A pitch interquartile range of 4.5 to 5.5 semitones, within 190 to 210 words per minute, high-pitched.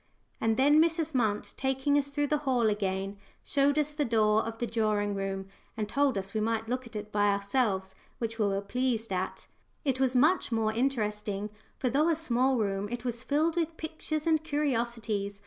Yes: average, 5.2 semitones; average, 195 wpm; high, 235 Hz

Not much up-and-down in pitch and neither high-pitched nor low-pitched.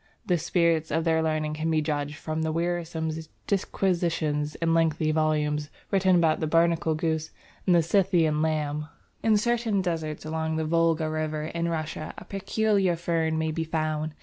Yes: narrow, 1.5 semitones; medium, 160 Hz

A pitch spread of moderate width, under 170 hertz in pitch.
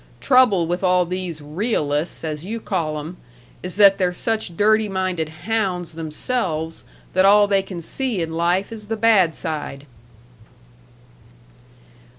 No: average, 4.2 semitones; medium, 185 Hz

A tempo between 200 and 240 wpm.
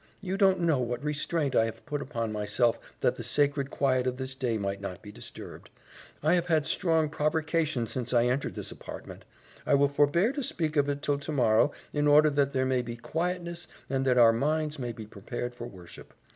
Yes: fast, 205 wpm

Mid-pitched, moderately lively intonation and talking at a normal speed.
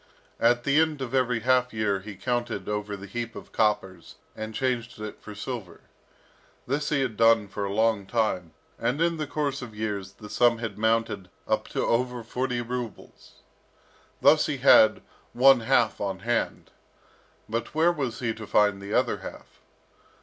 No: low, 115 Hz; average, 3.2 semitones; average, 170 wpm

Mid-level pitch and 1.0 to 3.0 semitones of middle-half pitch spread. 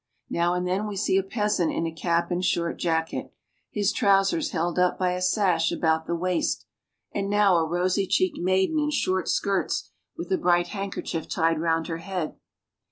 Yes: medium, 180 Hz; average, 2.7 semitones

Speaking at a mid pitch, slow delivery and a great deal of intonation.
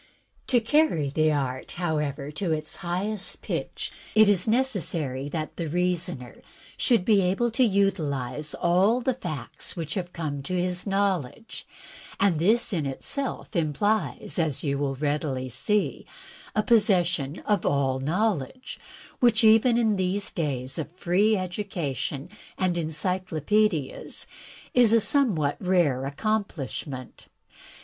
Yes: medium, 175 Hz; slow, 130 wpm; wide, 6.2 semitones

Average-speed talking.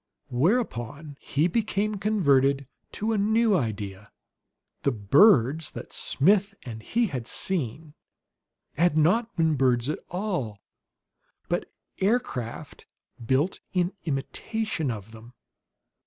No: slow, 110 wpm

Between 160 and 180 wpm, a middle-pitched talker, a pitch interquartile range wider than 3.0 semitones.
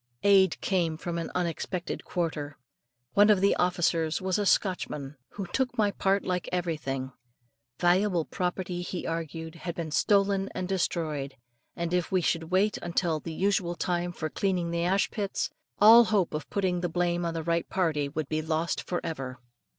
No: average, 170 wpm; medium, 175 Hz; average, 2.7 semitones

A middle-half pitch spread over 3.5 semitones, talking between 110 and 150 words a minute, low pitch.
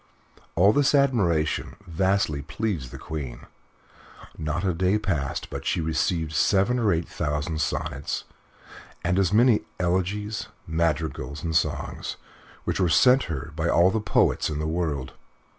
Yes: average, 4.3 semitones; average, 140 wpm; very low, 85 Hz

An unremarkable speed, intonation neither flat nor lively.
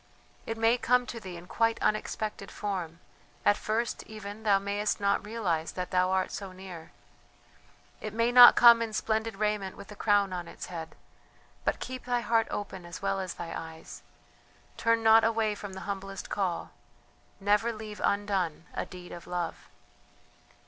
Yes: average, 170 wpm; average, 3.3 semitones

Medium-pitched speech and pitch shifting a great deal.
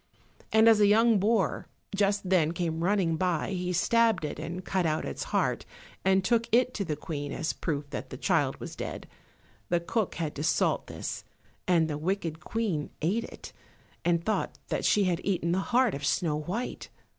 No: medium, 180 Hz; average, 4.3 semitones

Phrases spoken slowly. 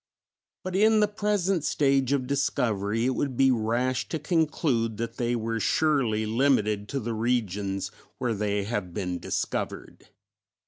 No: average, 145 wpm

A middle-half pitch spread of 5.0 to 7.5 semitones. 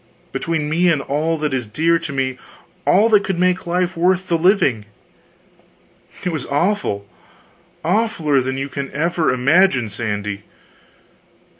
Yes: average, 5.3 semitones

